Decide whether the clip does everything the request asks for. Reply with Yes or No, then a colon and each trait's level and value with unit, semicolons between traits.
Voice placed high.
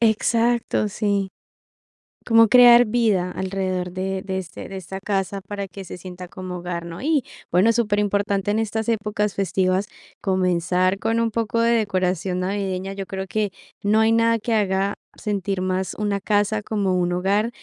Yes: high, 200 Hz